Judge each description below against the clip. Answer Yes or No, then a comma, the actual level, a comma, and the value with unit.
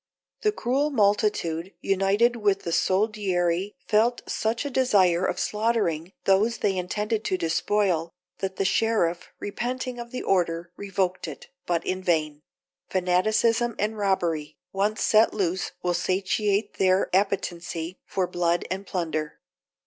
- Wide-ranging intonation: No, average, 3.5 semitones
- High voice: Yes, high, 195 Hz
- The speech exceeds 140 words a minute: No, slow, 135 wpm